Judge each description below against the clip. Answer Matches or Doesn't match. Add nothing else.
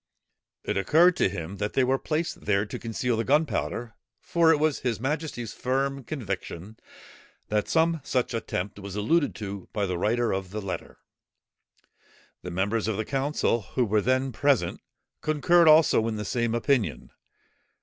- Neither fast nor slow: Matches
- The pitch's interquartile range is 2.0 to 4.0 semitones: Doesn't match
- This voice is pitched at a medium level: Doesn't match